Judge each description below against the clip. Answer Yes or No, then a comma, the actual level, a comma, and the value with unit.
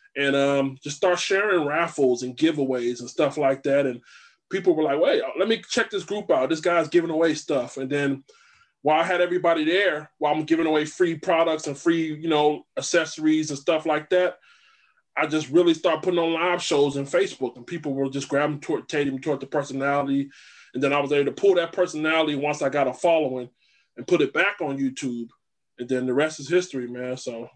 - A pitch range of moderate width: Yes, average, 3.6 semitones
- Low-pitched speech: No, medium, 150 Hz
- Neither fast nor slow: No, fast, 215 wpm